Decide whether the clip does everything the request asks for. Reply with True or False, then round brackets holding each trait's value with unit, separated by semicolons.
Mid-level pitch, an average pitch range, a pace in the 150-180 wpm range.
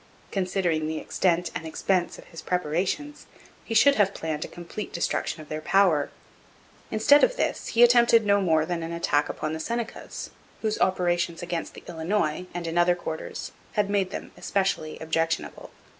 True (175 Hz; 3.8 semitones; 170 wpm)